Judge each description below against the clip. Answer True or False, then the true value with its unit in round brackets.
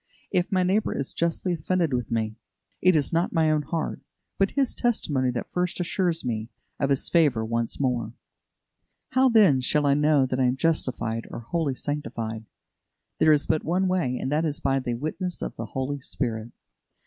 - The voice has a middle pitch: True (145 Hz)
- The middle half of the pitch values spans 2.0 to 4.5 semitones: False (5.4 semitones)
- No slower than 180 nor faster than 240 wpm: True (185 wpm)